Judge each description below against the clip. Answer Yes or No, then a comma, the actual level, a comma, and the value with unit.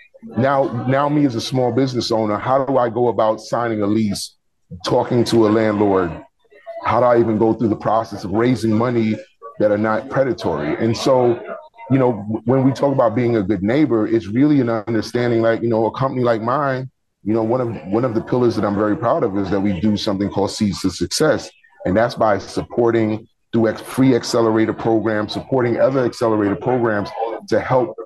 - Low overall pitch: Yes, low, 115 Hz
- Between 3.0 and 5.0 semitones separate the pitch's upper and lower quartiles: No, narrow, 2.6 semitones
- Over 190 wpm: Yes, average, 200 wpm